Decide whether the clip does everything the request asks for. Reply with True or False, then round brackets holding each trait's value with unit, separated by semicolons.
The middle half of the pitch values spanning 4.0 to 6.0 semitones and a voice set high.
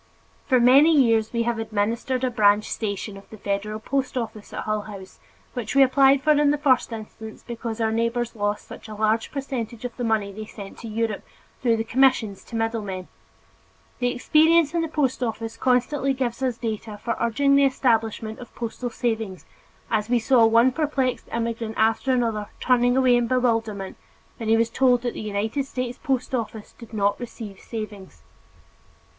False (2.8 semitones; 230 Hz)